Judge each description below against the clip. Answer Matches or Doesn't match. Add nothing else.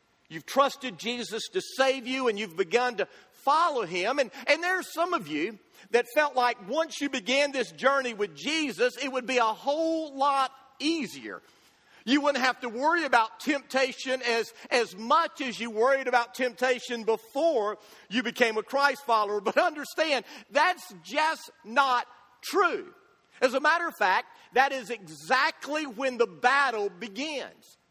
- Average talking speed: Matches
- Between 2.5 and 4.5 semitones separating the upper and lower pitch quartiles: Matches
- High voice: Matches